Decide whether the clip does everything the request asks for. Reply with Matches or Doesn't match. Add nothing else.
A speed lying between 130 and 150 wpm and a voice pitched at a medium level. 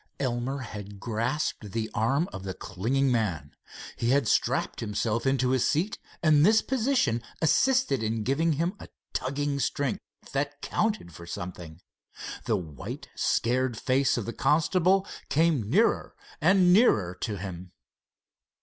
Doesn't match